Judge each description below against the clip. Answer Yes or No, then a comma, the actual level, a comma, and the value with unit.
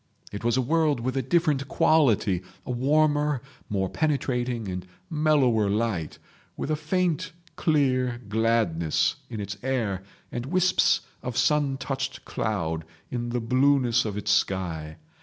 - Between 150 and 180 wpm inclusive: No, average, 140 wpm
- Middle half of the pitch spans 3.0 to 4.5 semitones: No, wide, 5.5 semitones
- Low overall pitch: Yes, low, 125 Hz